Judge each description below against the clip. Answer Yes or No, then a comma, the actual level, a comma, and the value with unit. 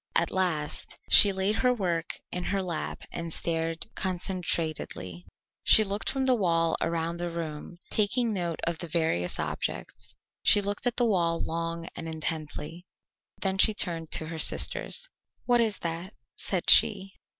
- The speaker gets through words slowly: No, average, 155 wpm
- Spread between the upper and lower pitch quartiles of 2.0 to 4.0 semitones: Yes, average, 3.4 semitones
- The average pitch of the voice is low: No, medium, 170 Hz